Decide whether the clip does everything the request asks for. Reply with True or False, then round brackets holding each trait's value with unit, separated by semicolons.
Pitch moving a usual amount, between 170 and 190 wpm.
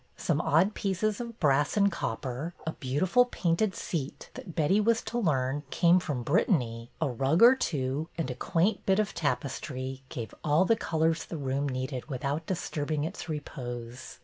False (5.8 semitones; 175 wpm)